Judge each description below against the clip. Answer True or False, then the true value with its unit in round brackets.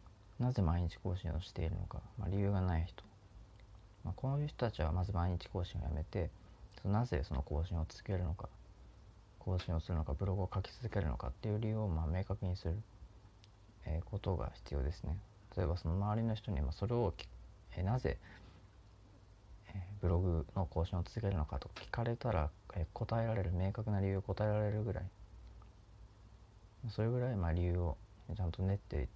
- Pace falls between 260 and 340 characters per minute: True (310 characters per minute)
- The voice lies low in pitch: True (95 Hz)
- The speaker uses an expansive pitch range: False (3.0 semitones)